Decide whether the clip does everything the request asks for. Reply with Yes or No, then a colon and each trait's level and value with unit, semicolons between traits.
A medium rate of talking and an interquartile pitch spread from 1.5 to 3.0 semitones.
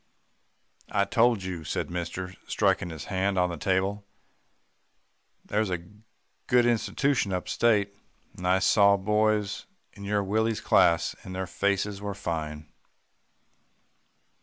No: slow, 130 wpm; narrow, 2.5 semitones